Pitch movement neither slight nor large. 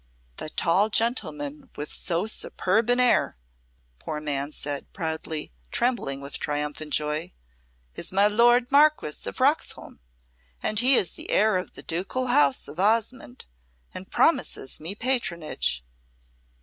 No: wide, 7.5 semitones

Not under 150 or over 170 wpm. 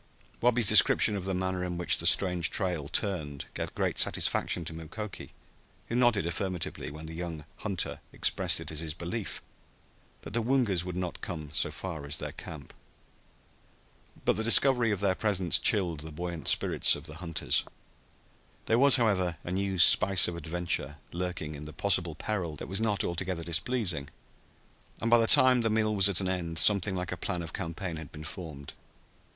No: average, 180 wpm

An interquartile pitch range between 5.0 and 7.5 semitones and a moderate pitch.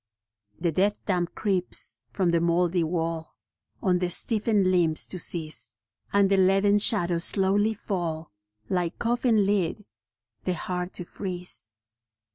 No: average, 2.9 semitones; medium, 180 Hz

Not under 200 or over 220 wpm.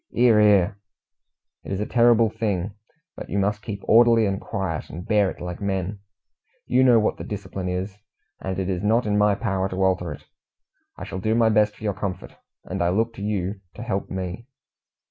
Yes: fast, 205 wpm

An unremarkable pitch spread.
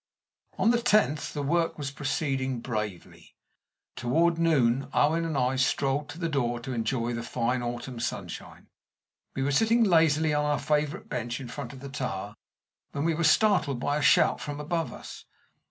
Yes: average, 4.4 semitones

